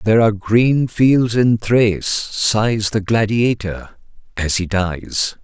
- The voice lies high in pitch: No, low, 110 Hz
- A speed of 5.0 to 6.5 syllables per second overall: No, 3.5 syllables/s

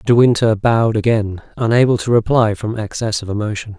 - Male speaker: Yes, male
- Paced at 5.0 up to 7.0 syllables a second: Yes, 5.5 syllables/s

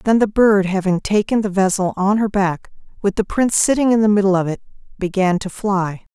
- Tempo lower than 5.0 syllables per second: No, 5.4 syllables/s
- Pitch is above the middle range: Yes, high, 200 Hz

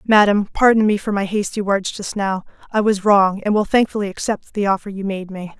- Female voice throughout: Yes, female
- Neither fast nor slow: No, fast, 225 wpm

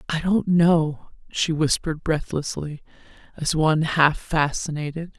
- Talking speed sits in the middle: No, slow, 115 wpm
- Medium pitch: Yes, medium, 155 Hz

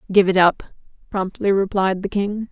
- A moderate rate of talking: Yes, average, 165 wpm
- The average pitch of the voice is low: No, high, 195 Hz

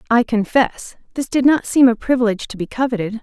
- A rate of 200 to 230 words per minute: Yes, fast, 205 wpm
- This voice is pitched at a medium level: No, high, 235 Hz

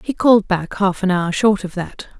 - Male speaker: No, female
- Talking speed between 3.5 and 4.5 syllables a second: No, 5.0 syllables/s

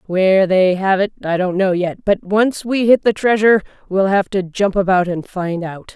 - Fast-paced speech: Yes, fast, 220 wpm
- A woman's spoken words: Yes, female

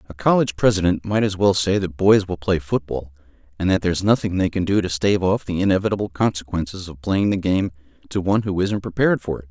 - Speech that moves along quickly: Yes, fast, 225 wpm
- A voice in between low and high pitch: No, very low, 95 Hz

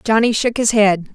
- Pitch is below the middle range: No, high, 220 Hz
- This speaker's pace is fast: Yes, fast, 210 wpm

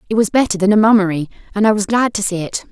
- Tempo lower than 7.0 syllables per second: No, 7.2 syllables/s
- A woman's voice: Yes, female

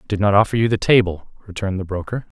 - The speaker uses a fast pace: Yes, fast, 250 wpm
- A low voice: Yes, low, 100 Hz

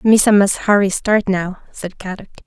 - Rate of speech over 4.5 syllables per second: Yes, 4.8 syllables/s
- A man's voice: No, female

